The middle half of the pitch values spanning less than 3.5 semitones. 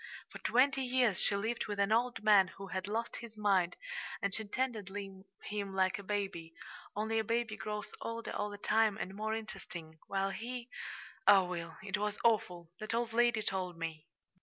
Yes: average, 2.7 semitones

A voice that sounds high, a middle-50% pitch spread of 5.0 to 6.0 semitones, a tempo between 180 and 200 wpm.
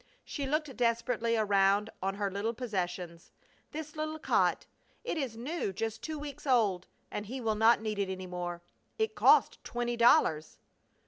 No: high, 225 Hz; average, 5.3 semitones; average, 165 wpm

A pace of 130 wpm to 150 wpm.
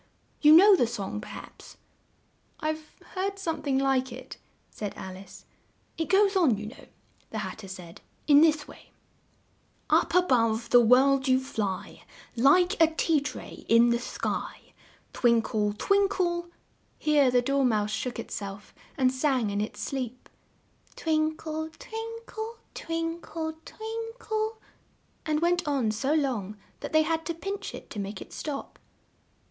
No: average, 165 wpm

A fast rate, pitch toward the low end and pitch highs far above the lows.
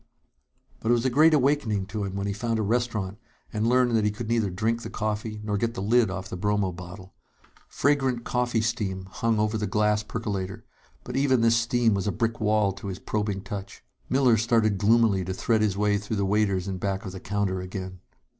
No: fast, 220 wpm; low, 105 Hz; average, 2.9 semitones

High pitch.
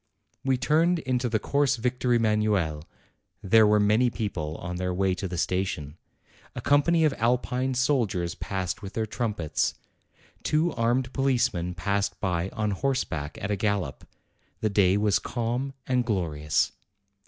No: low, 105 Hz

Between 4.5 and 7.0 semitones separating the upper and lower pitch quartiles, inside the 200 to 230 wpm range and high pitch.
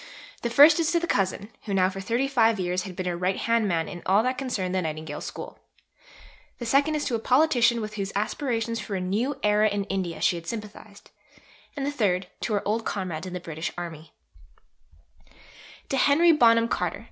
Yes: average, 4.9 semitones; fast, 205 wpm; high, 210 Hz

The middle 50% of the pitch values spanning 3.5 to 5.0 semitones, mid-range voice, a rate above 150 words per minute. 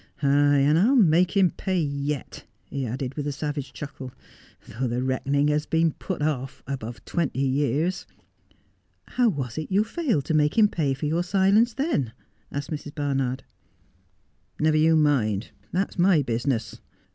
Yes: average, 4.3 semitones; medium, 145 Hz; average, 170 wpm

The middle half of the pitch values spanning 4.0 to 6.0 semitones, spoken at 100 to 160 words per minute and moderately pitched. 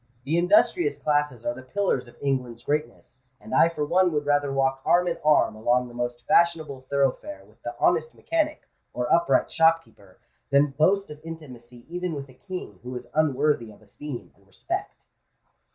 No: average, 4.9 semitones; average, 175 wpm; medium, 145 Hz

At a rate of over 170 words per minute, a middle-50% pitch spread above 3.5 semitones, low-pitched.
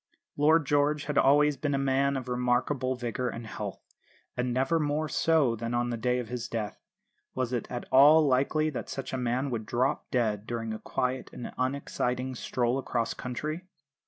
No: average, 185 wpm; average, 2.9 semitones; low, 130 Hz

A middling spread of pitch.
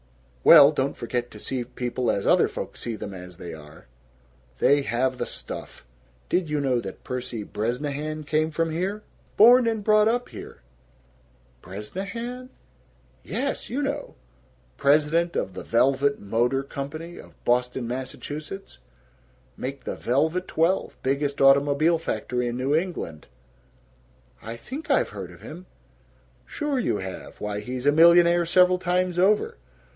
No: wide, 6.5 semitones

